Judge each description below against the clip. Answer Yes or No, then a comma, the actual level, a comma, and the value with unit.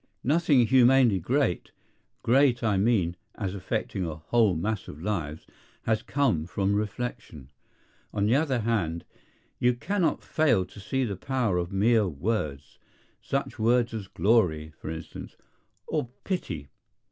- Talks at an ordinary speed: No, slow, 130 wpm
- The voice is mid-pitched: No, low, 105 Hz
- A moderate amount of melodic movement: No, wide, 5.8 semitones